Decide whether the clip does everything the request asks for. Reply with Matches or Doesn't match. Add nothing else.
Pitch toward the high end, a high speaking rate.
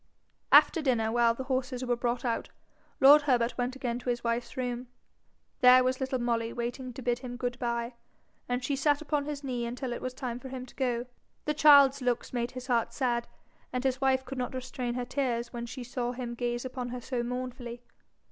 Matches